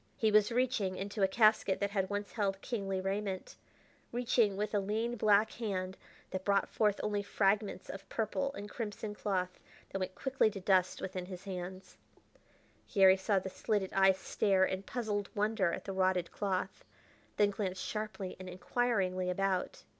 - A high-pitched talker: Yes, high, 200 Hz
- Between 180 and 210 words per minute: No, average, 165 wpm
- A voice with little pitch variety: Yes, narrow, 2.1 semitones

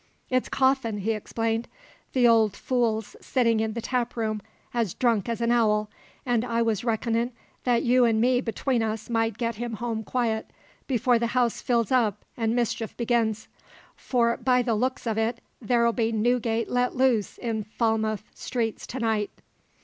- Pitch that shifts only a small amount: Yes, narrow, 1.7 semitones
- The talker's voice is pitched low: No, high, 230 Hz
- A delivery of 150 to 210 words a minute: Yes, average, 165 wpm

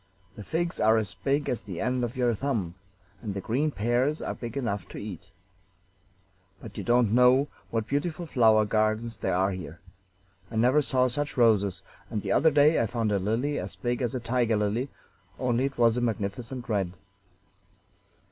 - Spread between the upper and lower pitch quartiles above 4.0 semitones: No, average, 3.5 semitones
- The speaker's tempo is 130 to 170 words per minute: No, average, 185 wpm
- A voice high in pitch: No, low, 115 Hz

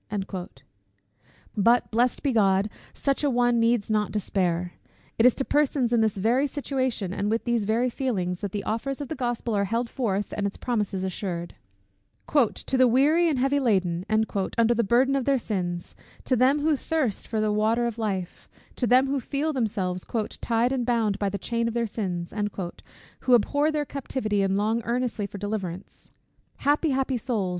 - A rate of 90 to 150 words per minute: No, average, 180 wpm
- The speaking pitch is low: No, high, 230 Hz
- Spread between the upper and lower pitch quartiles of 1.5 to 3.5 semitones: No, average, 4.2 semitones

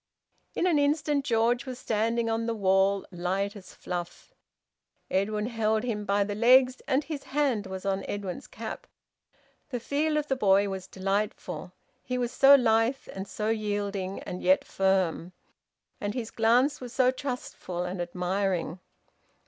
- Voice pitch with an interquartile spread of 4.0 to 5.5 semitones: Yes, average, 4.6 semitones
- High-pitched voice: Yes, high, 215 Hz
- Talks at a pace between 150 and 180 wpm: Yes, average, 155 wpm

